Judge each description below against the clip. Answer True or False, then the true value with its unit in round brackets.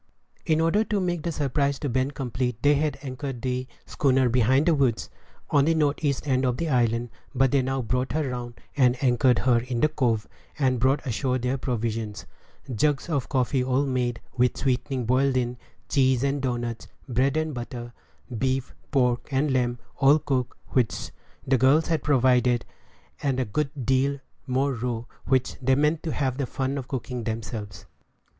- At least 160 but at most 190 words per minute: True (180 wpm)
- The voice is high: False (130 Hz)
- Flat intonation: True (2.3 semitones)